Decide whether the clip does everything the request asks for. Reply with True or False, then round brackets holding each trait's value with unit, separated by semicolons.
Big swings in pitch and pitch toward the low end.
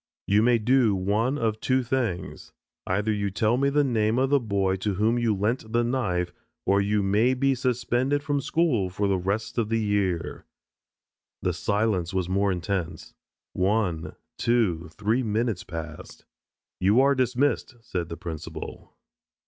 False (4.4 semitones; 105 Hz)